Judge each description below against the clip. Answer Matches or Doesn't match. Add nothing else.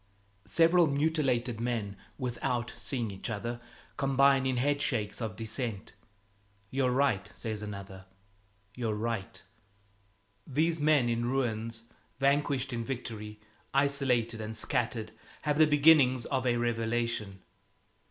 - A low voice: Matches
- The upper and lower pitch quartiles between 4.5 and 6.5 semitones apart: Doesn't match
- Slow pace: Matches